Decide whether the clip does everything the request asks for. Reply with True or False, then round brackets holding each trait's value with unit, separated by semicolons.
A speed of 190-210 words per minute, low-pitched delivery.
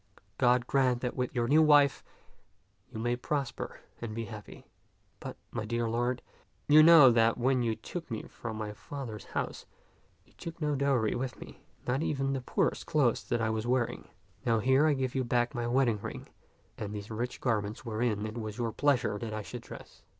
True (195 wpm; 120 Hz)